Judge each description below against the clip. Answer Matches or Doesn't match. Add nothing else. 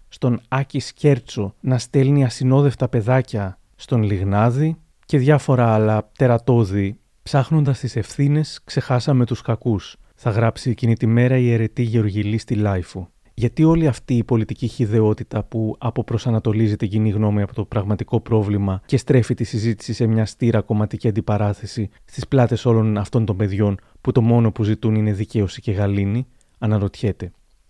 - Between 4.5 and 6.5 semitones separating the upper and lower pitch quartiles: Doesn't match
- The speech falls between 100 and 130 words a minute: Doesn't match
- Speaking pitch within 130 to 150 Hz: Doesn't match